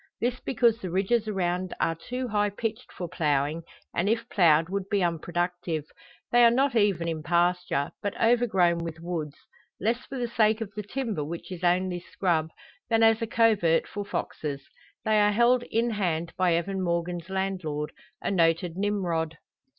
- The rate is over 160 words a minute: Yes, average, 170 wpm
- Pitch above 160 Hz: Yes, medium, 185 Hz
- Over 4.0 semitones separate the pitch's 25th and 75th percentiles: Yes, average, 4.6 semitones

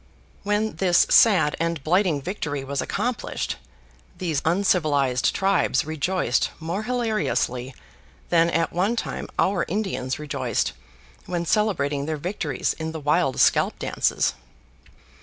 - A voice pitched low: No, medium, 165 Hz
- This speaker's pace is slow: Yes, slow, 120 wpm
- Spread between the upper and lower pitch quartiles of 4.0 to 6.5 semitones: Yes, average, 5.2 semitones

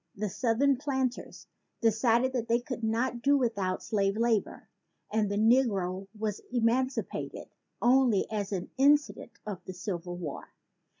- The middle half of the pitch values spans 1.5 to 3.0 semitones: No, average, 4.2 semitones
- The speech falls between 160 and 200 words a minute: No, slow, 135 wpm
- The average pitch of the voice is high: Yes, high, 225 Hz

